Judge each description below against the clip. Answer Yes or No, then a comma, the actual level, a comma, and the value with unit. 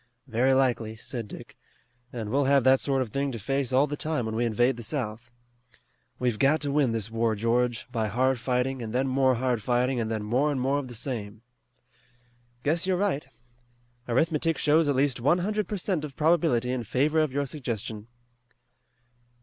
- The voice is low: Yes, low, 130 Hz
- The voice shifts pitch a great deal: No, average, 3.6 semitones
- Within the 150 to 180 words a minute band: No, average, 190 wpm